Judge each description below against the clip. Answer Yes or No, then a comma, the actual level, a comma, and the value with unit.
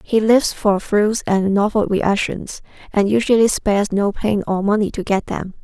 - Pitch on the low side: No, high, 205 Hz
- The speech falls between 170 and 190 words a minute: Yes, average, 180 wpm